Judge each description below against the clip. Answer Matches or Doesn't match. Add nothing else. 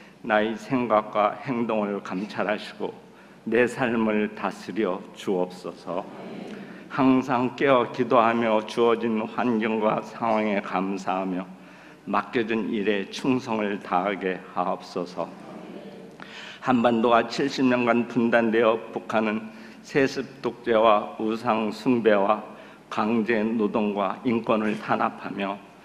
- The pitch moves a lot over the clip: Doesn't match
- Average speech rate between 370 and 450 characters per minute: Doesn't match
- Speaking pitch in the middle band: Doesn't match